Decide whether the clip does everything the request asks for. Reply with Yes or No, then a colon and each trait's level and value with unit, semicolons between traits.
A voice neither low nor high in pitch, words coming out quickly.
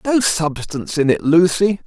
No: medium, 165 Hz; average, 160 wpm